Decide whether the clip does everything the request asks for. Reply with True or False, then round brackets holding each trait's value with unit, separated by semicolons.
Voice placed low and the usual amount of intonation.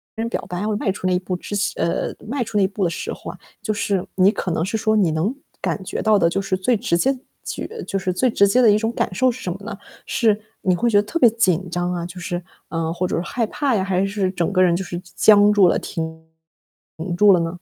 False (195 Hz; 3.4 semitones)